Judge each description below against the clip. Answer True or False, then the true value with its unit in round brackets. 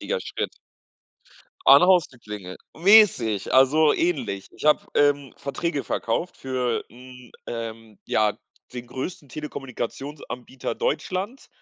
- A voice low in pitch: True (130 Hz)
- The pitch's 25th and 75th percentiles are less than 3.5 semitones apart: False (5.0 semitones)